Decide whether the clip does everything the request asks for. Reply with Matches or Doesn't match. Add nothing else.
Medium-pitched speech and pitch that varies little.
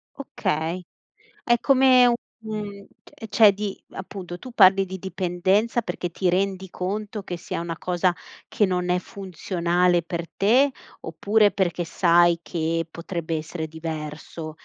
Doesn't match